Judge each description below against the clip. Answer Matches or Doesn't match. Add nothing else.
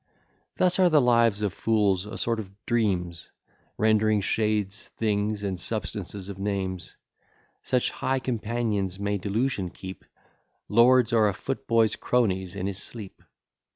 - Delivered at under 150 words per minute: Matches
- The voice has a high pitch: Doesn't match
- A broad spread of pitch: Doesn't match